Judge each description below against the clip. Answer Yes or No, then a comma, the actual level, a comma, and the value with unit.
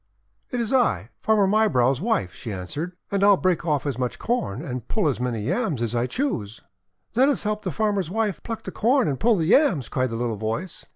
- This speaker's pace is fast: Yes, fast, 230 wpm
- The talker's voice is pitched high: No, medium, 170 Hz